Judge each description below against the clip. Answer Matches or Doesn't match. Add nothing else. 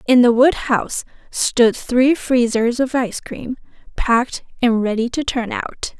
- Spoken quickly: Doesn't match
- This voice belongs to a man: Doesn't match